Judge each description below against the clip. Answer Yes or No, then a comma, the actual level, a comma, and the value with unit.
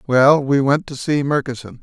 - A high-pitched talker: No, low, 135 Hz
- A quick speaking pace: No, average, 195 wpm